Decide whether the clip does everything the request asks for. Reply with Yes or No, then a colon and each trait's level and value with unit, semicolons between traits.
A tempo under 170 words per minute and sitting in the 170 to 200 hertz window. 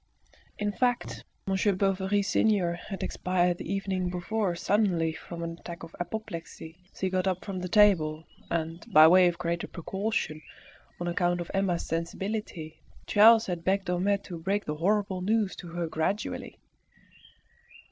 Yes: average, 150 wpm; medium, 185 Hz